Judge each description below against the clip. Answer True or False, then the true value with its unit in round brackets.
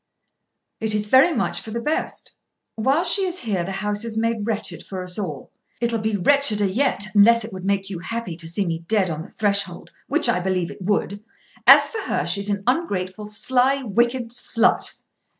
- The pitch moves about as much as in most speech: True (3.7 semitones)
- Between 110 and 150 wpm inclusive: False (195 wpm)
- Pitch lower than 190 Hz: False (210 Hz)